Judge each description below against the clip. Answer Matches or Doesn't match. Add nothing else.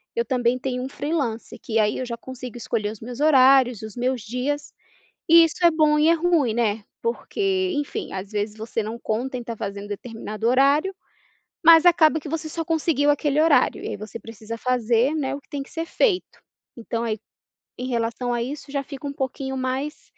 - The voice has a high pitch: Matches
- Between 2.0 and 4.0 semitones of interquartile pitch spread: Doesn't match